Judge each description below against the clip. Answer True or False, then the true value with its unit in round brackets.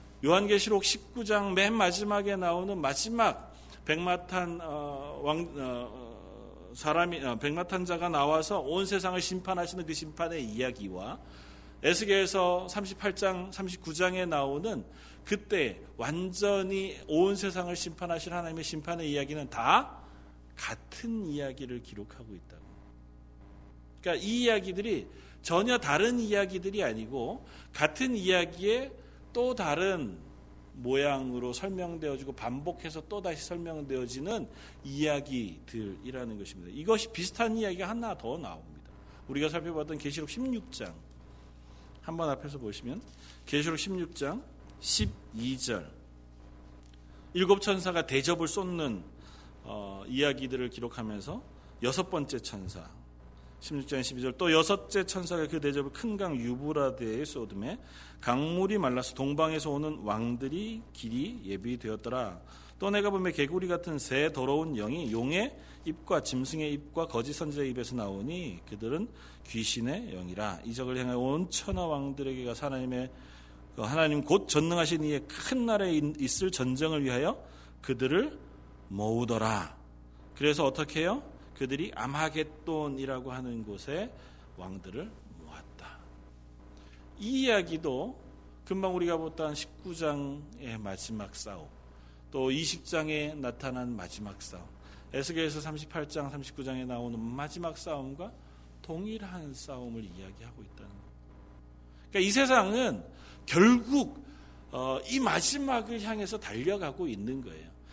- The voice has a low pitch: False (145 Hz)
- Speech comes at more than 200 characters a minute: True (270 characters per minute)